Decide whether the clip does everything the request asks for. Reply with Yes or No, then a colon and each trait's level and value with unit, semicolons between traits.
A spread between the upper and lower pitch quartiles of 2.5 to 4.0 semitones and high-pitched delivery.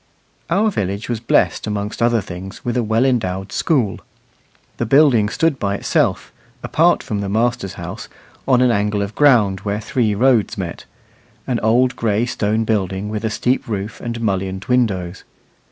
No: average, 3.4 semitones; low, 110 Hz